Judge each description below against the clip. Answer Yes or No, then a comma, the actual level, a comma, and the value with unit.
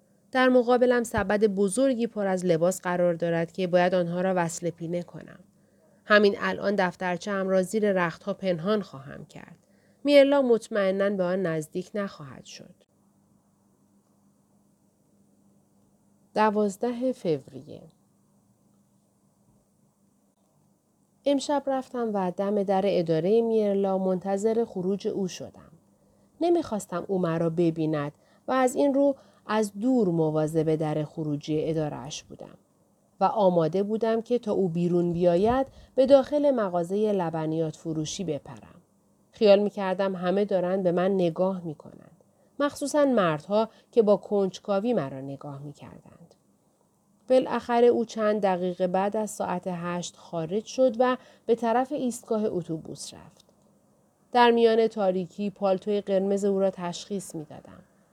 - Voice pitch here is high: Yes, high, 195 Hz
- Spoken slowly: No, average, 125 wpm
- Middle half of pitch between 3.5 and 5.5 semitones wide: Yes, average, 4.1 semitones